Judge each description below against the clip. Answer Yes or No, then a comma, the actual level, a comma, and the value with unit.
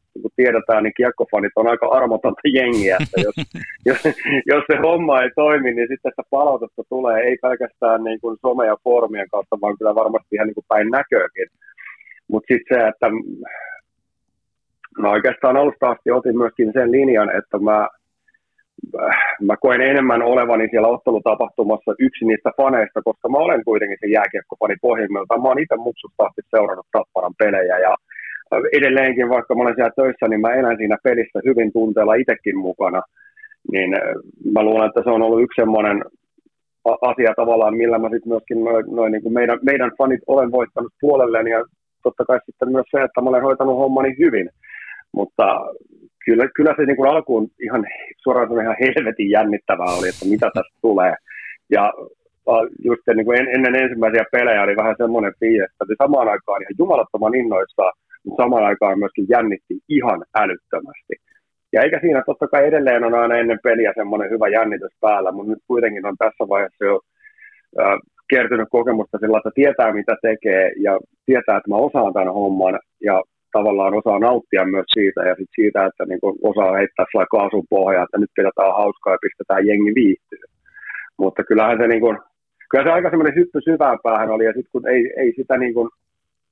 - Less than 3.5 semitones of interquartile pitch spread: No, average, 4.4 semitones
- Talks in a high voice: No, low, 120 Hz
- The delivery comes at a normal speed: No, fast, 170 wpm